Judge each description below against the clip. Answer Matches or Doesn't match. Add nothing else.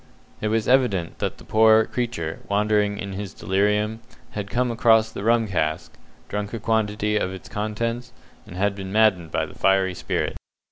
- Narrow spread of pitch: Matches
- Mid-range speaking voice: Doesn't match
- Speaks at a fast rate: Doesn't match